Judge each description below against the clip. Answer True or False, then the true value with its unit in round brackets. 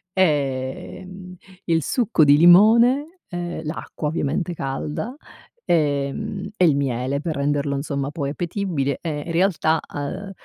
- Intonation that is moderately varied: True (4.8 semitones)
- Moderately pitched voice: True (160 Hz)